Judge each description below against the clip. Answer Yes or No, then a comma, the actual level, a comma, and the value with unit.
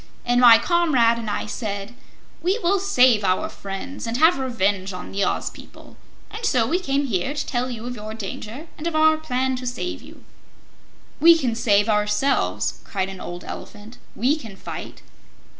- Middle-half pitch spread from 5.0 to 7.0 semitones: Yes, wide, 5.5 semitones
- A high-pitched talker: Yes, high, 245 Hz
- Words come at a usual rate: Yes, average, 180 wpm